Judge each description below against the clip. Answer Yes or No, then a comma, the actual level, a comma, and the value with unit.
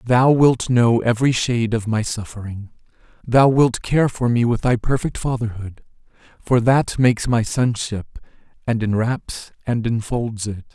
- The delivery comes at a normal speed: Yes, average, 150 wpm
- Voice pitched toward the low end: Yes, low, 115 Hz